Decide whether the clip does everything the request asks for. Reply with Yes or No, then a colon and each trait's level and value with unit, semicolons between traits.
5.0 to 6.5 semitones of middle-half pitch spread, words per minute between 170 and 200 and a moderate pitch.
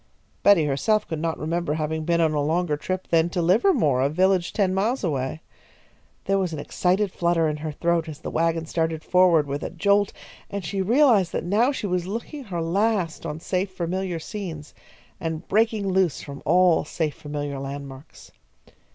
No: average, 3.6 semitones; average, 180 wpm; medium, 170 Hz